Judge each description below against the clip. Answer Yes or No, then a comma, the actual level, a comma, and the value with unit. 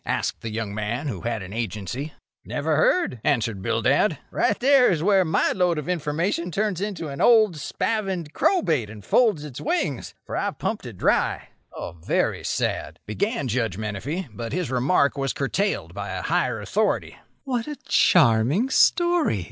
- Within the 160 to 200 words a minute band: Yes, average, 165 wpm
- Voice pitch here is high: No, medium, 150 Hz